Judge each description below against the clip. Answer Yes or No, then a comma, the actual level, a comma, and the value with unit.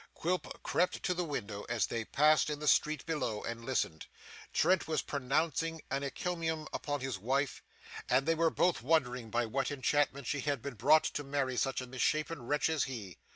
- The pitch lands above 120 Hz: Yes, medium, 140 Hz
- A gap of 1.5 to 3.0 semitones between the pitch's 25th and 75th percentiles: No, average, 3.9 semitones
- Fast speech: No, average, 190 wpm